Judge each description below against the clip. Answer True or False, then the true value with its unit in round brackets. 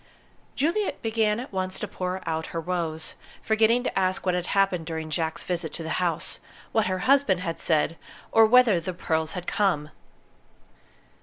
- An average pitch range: True (4.5 semitones)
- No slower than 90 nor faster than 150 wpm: False (170 wpm)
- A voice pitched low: False (185 Hz)